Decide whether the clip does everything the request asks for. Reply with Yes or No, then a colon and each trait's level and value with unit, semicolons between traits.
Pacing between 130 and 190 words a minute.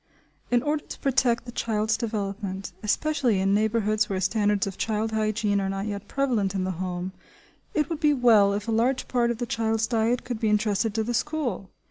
No: average, 200 wpm